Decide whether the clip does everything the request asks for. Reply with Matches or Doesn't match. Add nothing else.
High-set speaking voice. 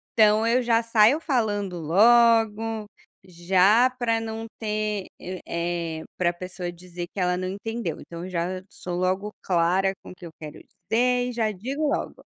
Matches